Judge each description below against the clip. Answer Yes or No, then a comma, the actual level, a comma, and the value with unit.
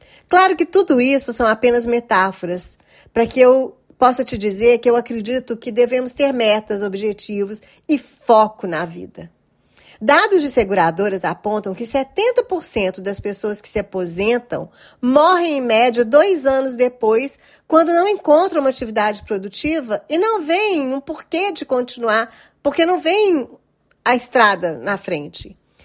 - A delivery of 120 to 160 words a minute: Yes, average, 145 wpm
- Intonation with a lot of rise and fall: Yes, wide, 5.9 semitones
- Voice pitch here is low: No, high, 245 Hz